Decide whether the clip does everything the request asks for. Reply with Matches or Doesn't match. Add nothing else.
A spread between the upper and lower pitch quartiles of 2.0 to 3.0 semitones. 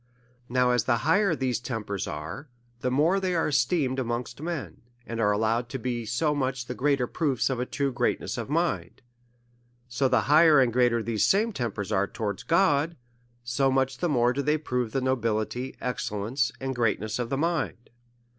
Doesn't match